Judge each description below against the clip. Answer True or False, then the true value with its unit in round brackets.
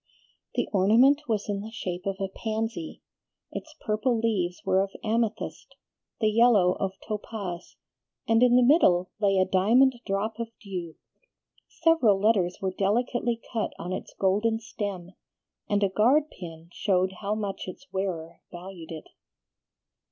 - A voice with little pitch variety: False (3.4 semitones)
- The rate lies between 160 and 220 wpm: False (145 wpm)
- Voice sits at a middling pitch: False (205 Hz)